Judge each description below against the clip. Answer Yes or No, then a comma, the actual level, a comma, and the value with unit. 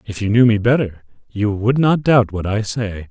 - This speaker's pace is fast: Yes, fast, 230 wpm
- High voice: No, low, 110 Hz